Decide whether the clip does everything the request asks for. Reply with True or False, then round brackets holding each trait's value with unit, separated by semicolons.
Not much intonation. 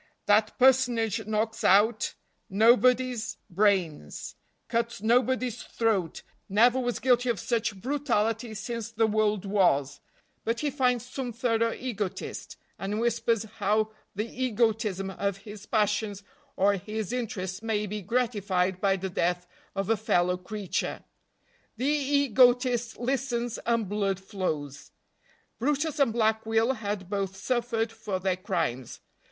False (3.4 semitones)